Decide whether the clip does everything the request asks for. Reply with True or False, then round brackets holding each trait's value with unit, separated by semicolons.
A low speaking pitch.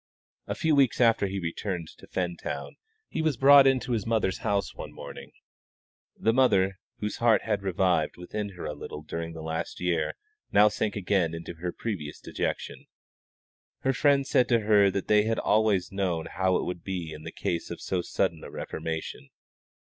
True (95 Hz)